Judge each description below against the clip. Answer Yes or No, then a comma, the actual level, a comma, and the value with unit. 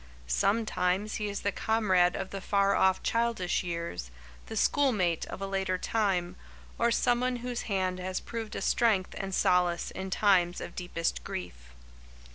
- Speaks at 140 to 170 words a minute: Yes, average, 155 wpm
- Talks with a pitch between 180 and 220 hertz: Yes, high, 190 Hz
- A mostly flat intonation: No, average, 3.3 semitones